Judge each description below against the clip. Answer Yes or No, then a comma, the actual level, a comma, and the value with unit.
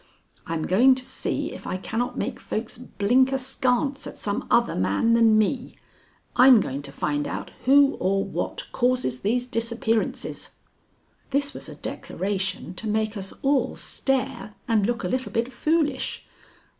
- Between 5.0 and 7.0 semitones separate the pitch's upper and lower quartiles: No, average, 4.4 semitones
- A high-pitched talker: Yes, high, 230 Hz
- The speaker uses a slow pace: No, average, 155 wpm